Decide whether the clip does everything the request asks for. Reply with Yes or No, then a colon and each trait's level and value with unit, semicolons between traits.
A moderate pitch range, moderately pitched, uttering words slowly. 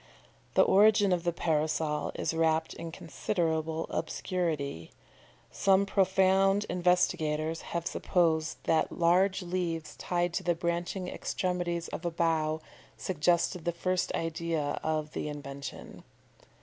No: narrow, 2.3 semitones; medium, 170 Hz; slow, 120 wpm